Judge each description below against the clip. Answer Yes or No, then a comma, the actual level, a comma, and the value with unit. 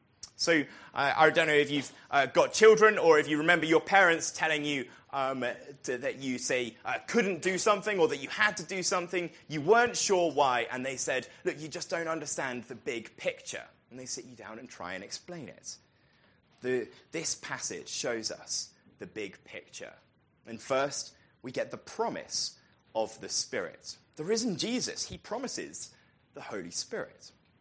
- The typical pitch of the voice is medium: Yes, medium, 155 Hz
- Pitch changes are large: Yes, wide, 5.8 semitones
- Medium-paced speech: Yes, average, 185 wpm